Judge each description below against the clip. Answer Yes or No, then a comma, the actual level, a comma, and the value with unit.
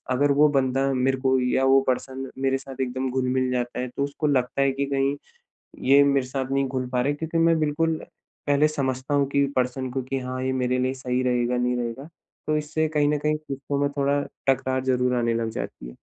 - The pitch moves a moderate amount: No, narrow, 1.9 semitones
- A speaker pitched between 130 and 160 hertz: Yes, low, 135 Hz